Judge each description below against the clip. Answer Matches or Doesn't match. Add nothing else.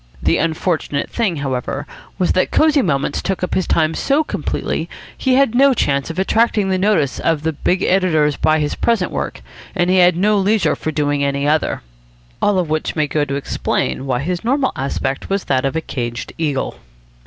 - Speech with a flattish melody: Doesn't match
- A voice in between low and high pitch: Matches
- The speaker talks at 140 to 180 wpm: Doesn't match